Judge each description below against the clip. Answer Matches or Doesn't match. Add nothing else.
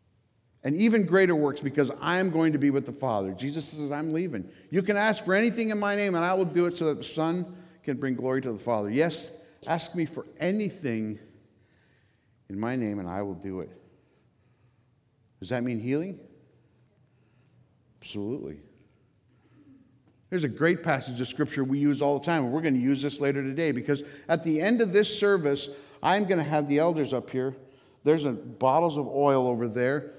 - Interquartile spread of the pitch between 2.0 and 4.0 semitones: Doesn't match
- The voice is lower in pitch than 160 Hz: Matches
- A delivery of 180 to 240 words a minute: Matches